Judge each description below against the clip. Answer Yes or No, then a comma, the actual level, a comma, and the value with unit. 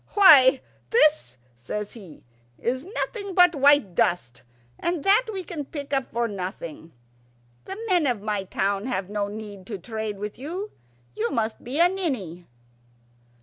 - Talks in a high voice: Yes, high, 235 Hz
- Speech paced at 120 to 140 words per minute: No, average, 150 wpm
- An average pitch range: No, wide, 8.1 semitones